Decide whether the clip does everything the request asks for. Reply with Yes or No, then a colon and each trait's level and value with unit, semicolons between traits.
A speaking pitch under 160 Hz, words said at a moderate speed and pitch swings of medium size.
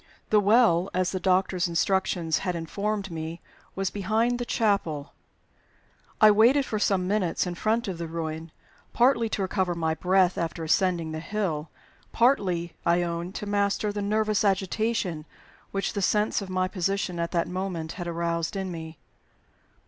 No: medium, 185 Hz; average, 160 wpm; average, 3.5 semitones